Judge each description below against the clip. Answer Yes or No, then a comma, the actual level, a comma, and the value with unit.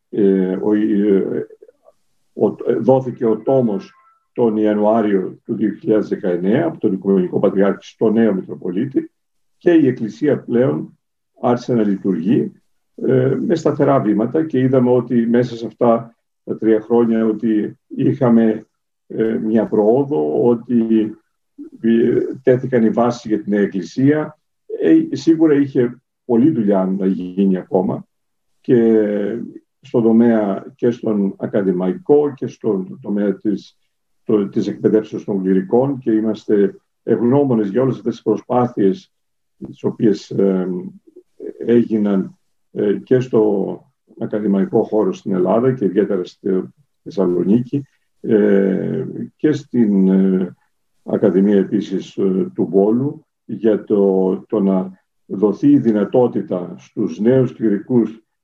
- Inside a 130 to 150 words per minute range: No, slow, 115 wpm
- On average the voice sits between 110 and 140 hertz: Yes, low, 115 Hz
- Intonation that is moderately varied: Yes, average, 4.2 semitones